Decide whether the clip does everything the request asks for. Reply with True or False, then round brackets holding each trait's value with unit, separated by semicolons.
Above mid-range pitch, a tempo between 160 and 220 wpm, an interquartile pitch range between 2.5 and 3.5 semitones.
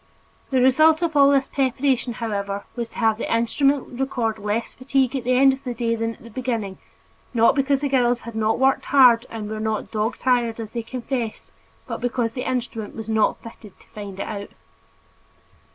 True (235 Hz; 200 wpm; 3.0 semitones)